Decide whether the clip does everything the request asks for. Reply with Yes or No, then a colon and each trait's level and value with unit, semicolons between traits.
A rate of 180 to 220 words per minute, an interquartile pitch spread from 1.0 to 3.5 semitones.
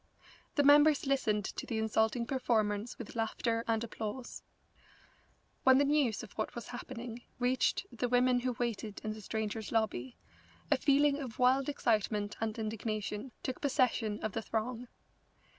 No: average, 145 wpm; average, 3.0 semitones